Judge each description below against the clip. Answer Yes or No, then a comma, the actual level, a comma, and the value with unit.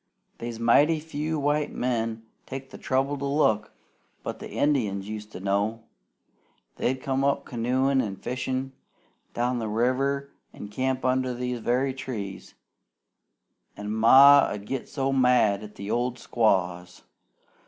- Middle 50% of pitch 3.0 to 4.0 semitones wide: Yes, average, 3.7 semitones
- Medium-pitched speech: No, low, 125 Hz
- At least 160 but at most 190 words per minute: No, slow, 135 wpm